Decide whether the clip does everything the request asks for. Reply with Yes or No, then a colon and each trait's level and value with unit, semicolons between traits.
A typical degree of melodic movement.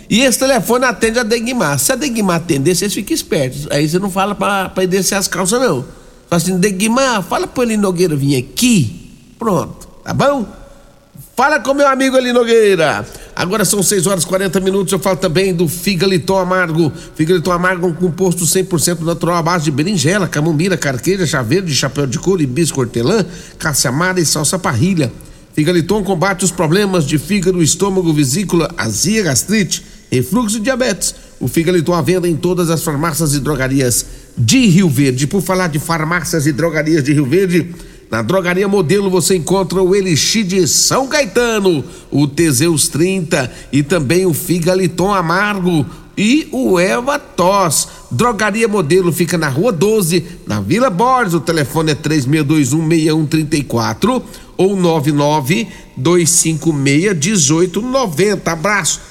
Yes: average, 3.7 semitones